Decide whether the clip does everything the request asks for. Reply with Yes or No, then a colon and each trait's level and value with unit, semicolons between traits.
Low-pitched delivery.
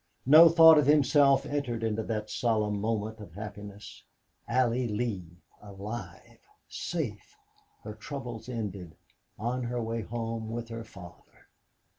Yes: low, 115 Hz